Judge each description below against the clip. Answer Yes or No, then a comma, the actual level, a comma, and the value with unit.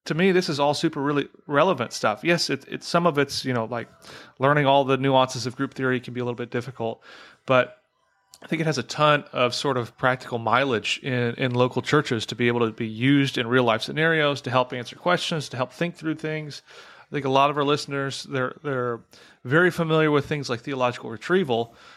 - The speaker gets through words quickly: Yes, fast, 225 wpm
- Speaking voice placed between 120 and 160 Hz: Yes, low, 135 Hz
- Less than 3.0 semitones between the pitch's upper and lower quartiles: No, average, 3.4 semitones